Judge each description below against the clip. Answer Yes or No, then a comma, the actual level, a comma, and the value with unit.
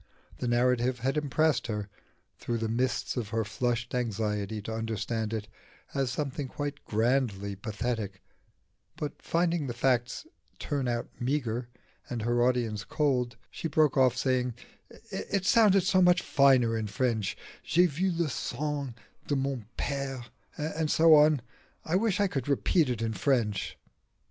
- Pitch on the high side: No, low, 125 Hz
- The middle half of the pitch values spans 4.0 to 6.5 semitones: Yes, average, 4.4 semitones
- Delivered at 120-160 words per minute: Yes, average, 150 wpm